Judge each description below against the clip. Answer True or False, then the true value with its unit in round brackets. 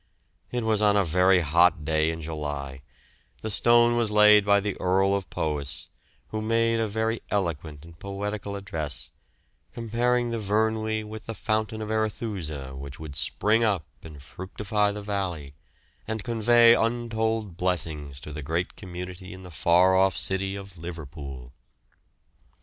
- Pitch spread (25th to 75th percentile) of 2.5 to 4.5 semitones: False (5.3 semitones)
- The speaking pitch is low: True (95 Hz)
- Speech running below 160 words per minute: True (150 wpm)